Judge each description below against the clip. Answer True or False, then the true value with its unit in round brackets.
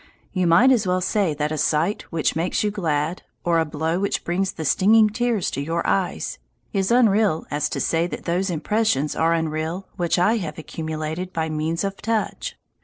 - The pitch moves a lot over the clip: False (3.9 semitones)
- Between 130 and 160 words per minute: False (190 wpm)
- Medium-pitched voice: True (170 Hz)